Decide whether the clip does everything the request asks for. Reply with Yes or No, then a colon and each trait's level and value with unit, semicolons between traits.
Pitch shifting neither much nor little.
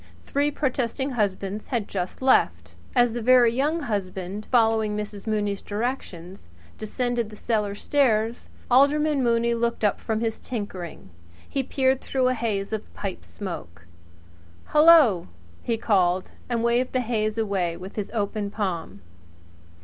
Yes: average, 3.7 semitones